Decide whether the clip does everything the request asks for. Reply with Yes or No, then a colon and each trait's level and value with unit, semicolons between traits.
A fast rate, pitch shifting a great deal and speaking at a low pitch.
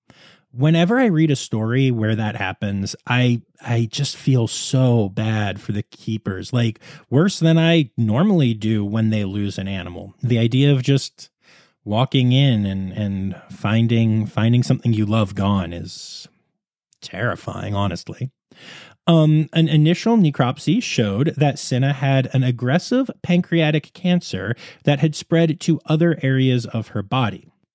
No: average, 145 wpm; wide, 6.3 semitones; low, 125 Hz